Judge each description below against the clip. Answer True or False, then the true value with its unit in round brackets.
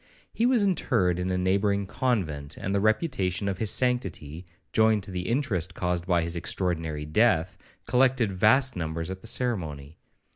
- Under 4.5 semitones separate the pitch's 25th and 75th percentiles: False (5.2 semitones)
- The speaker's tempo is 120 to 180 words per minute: True (160 wpm)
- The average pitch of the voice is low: True (95 Hz)